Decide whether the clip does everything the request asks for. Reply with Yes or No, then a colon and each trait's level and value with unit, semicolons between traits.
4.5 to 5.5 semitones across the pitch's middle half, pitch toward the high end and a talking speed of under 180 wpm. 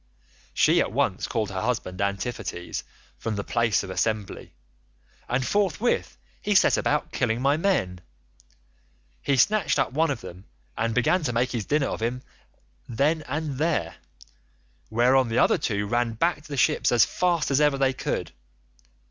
No: average, 5.0 semitones; low, 125 Hz; average, 165 wpm